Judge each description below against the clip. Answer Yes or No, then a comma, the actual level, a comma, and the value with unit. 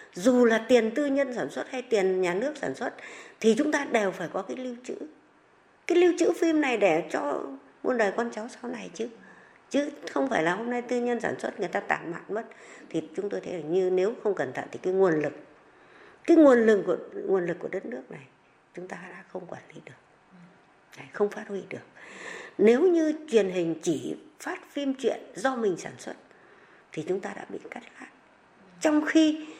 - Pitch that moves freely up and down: Yes, wide, 7.8 semitones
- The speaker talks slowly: No, average, 215 wpm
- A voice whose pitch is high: Yes, high, 230 Hz